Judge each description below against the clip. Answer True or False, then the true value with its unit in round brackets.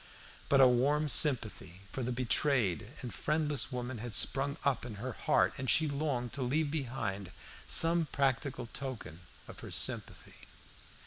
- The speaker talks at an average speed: True (150 wpm)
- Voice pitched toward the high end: False (130 Hz)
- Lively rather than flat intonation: False (3.0 semitones)